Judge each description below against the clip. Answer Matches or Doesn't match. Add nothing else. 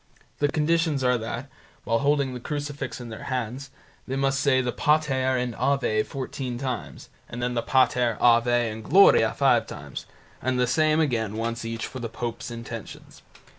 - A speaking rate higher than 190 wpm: Doesn't match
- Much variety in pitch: Doesn't match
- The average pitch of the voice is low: Matches